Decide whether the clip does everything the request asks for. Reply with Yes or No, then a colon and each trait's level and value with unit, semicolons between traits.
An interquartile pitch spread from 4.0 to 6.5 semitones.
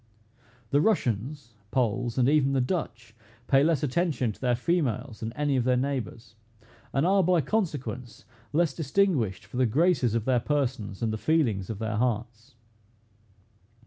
Yes: average, 4.4 semitones